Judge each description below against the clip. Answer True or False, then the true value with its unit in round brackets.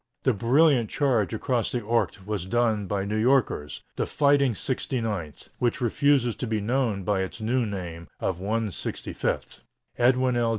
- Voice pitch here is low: True (115 Hz)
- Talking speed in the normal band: True (155 wpm)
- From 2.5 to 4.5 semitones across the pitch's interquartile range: True (3.9 semitones)